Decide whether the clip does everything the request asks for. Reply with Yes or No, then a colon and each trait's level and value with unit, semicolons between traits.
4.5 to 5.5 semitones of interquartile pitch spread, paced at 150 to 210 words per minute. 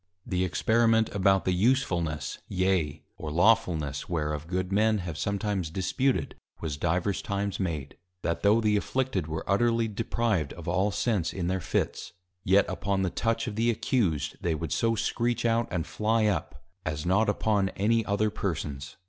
Yes: average, 4.8 semitones; average, 165 wpm